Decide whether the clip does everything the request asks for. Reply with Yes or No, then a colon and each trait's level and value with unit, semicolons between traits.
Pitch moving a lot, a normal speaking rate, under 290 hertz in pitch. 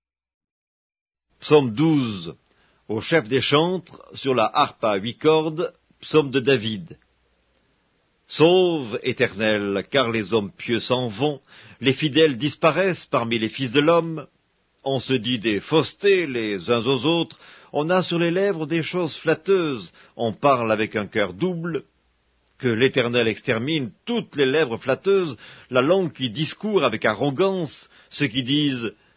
Yes: wide, 6.1 semitones; average, 145 wpm; low, 135 Hz